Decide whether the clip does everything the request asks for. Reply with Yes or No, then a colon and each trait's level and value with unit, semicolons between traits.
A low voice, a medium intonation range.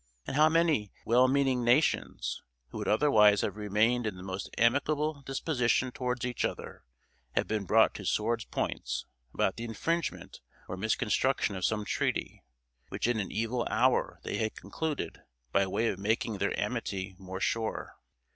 Yes: low, 115 Hz; average, 3.8 semitones